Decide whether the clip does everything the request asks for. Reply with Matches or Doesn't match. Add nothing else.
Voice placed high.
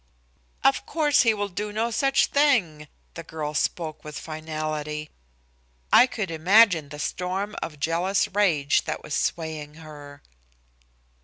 Doesn't match